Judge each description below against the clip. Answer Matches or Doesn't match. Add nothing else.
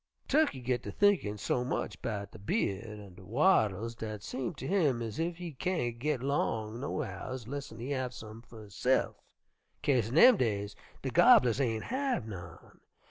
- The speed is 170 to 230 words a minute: Matches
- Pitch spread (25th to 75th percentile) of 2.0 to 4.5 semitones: Doesn't match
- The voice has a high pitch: Doesn't match